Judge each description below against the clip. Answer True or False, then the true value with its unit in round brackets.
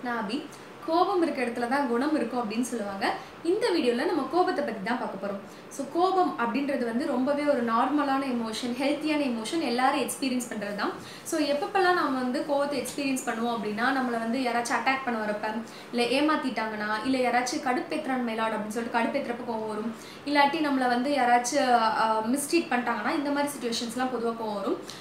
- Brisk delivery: True (160 wpm)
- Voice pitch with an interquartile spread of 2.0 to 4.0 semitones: True (3.5 semitones)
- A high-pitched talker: True (255 Hz)